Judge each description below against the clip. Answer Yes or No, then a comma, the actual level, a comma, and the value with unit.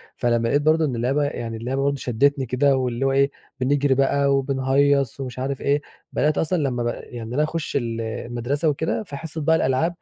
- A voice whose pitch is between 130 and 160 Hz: Yes, low, 135 Hz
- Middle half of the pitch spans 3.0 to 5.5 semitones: No, narrow, 2.6 semitones